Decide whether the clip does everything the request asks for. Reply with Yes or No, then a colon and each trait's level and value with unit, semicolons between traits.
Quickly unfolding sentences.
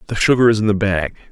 Yes: fast, 275 wpm